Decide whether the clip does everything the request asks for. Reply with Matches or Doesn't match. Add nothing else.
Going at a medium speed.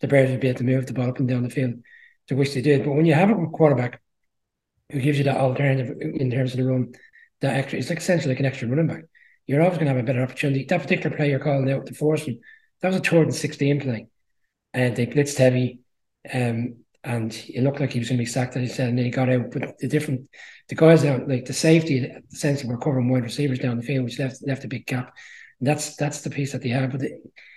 Doesn't match